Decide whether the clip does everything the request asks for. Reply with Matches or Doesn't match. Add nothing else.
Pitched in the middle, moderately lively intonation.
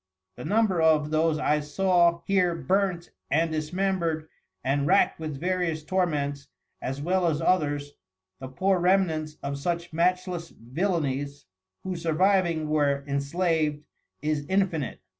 Matches